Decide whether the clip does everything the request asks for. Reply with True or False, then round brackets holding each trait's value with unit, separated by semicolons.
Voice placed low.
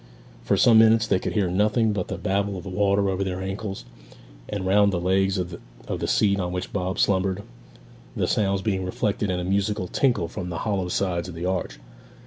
True (95 Hz)